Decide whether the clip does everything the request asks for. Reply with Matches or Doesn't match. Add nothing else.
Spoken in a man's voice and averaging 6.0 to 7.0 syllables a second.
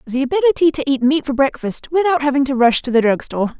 Doesn't match